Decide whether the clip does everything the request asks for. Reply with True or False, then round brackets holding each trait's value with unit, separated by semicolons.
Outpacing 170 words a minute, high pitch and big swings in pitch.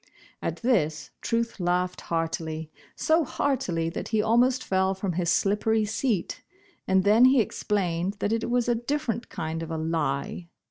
False (155 wpm; 200 Hz; 5.8 semitones)